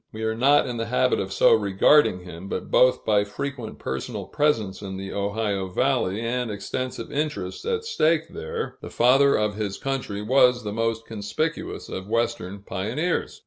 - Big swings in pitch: No, average, 4.3 semitones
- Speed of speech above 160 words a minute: Yes, average, 170 wpm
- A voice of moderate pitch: No, low, 110 Hz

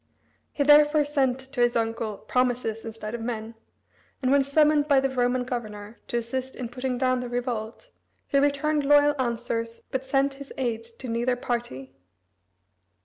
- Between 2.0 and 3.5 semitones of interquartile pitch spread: Yes, average, 3.0 semitones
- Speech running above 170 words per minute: No, average, 160 wpm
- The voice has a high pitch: Yes, very high, 250 Hz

